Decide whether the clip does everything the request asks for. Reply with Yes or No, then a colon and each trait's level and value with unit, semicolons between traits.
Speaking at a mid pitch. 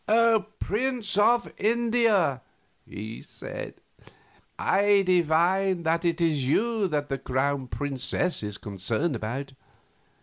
Yes: medium, 165 Hz